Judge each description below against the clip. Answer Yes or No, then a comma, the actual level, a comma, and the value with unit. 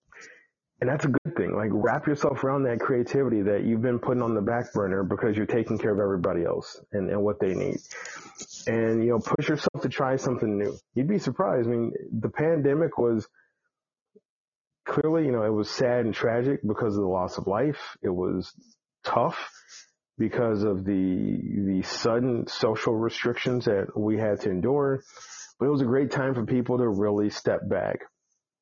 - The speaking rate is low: No, average, 185 wpm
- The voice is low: Yes, low, 115 Hz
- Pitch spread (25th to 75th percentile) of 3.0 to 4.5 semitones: Yes, average, 3.9 semitones